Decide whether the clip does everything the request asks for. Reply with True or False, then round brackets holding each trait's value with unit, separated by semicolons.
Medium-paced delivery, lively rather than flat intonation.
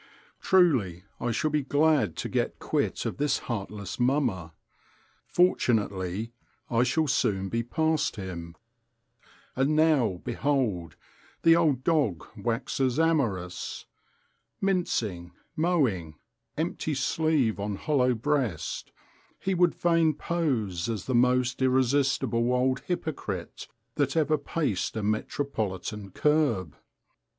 False (110 wpm; 7.0 semitones)